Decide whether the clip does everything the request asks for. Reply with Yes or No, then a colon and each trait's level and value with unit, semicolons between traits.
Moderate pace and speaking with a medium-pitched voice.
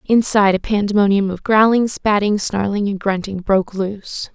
No: average, 150 wpm; high, 200 Hz